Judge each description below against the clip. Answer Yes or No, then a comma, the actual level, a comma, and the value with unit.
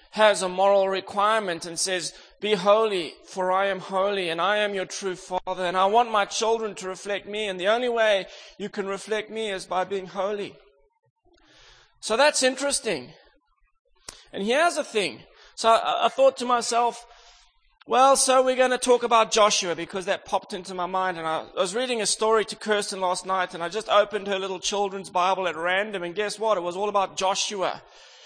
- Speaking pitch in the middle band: No, high, 205 Hz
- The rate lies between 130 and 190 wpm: No, average, 200 wpm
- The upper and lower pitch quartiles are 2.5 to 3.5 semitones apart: Yes, average, 3.2 semitones